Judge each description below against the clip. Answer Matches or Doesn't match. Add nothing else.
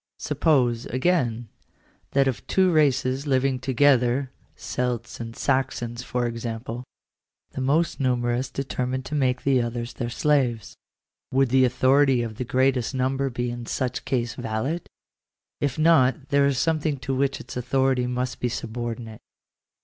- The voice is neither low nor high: Doesn't match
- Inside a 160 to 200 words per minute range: Doesn't match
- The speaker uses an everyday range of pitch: Doesn't match